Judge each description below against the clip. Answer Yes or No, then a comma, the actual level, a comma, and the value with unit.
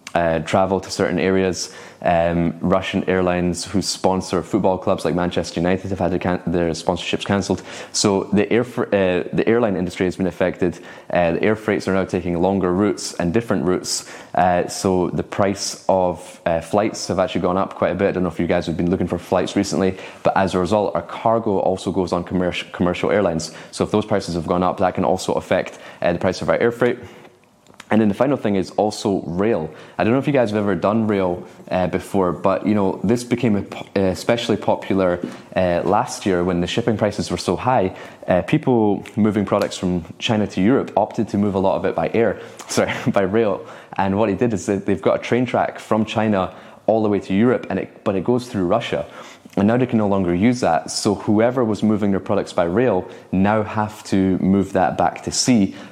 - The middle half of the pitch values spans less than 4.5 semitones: Yes, average, 2.7 semitones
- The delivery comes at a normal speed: No, fast, 220 wpm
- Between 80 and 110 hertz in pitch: Yes, very low, 95 Hz